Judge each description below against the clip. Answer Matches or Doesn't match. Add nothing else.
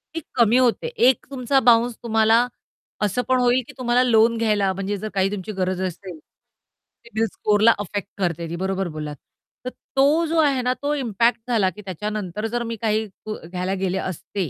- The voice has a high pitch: Matches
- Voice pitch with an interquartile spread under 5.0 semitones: Matches